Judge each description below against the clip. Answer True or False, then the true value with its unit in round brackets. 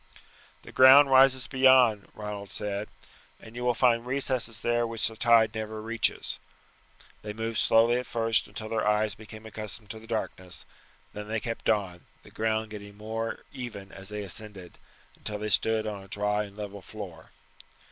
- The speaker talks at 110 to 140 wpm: False (170 wpm)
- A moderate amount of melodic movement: False (2.0 semitones)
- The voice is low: True (110 Hz)